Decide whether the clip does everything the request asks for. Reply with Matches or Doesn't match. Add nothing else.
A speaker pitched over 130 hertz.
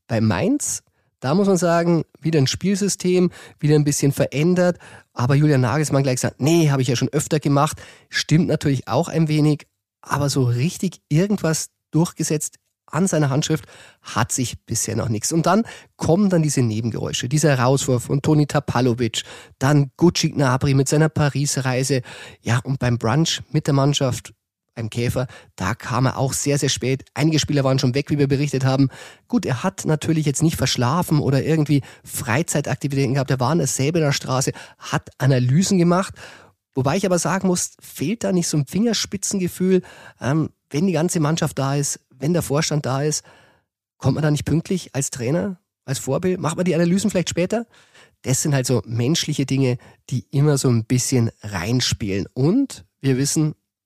Matches